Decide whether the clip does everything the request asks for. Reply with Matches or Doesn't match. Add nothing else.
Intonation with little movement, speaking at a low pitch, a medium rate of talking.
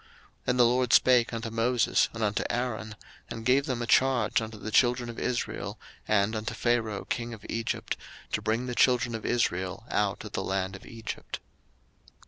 Matches